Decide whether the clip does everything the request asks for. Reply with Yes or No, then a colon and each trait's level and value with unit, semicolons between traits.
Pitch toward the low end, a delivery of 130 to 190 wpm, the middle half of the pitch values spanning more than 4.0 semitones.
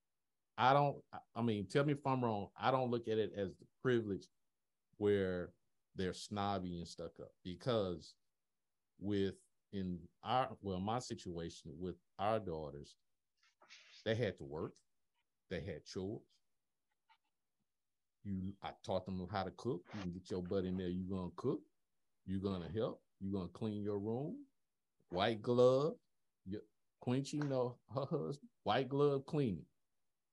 Yes: low, 100 Hz; average, 140 wpm; average, 5.0 semitones